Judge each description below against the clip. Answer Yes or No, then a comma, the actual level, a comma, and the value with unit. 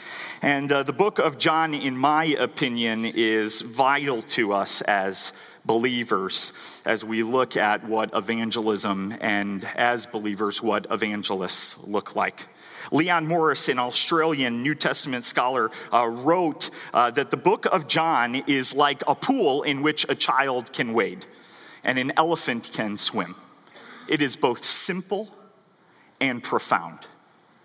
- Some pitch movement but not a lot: No, wide, 5.7 semitones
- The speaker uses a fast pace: No, average, 140 wpm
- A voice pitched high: No, low, 130 Hz